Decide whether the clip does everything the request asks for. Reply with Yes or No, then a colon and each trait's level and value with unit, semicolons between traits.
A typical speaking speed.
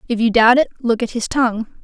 No: fast, 260 wpm